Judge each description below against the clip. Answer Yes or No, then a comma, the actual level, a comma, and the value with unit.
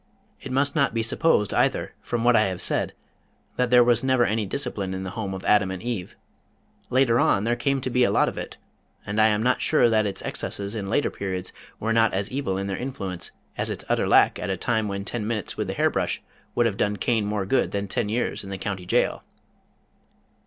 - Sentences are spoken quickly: Yes, fast, 230 wpm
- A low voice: Yes, low, 110 Hz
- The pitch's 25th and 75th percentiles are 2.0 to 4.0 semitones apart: Yes, average, 3.6 semitones